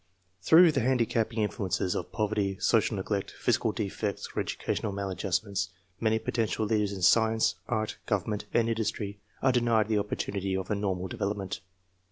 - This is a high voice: No, low, 105 Hz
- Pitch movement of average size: No, narrow, 2.2 semitones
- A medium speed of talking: Yes, average, 160 wpm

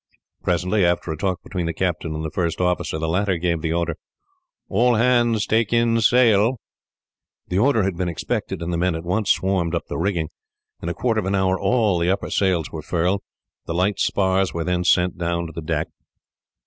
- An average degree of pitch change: Yes, average, 3.1 semitones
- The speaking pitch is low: Yes, very low, 90 Hz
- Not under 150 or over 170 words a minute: No, fast, 205 wpm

